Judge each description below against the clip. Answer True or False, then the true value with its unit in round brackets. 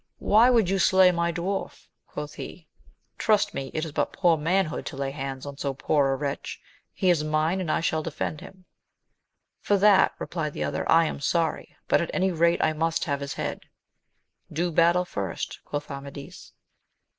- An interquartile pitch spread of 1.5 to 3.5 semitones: False (4.0 semitones)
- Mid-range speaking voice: True (165 Hz)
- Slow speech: False (185 wpm)